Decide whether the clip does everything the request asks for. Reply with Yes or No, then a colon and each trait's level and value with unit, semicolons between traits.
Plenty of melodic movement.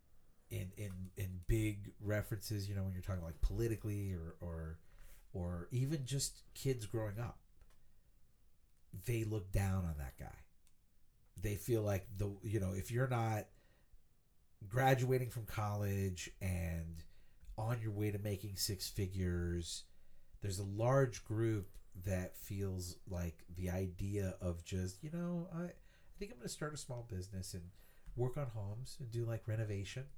No: average, 3.8 semitones